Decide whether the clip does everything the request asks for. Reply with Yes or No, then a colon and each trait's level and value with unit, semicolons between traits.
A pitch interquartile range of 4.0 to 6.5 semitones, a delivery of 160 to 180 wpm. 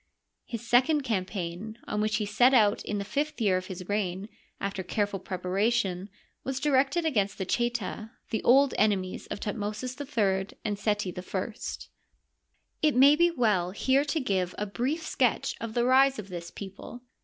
Yes: average, 4.8 semitones; average, 165 wpm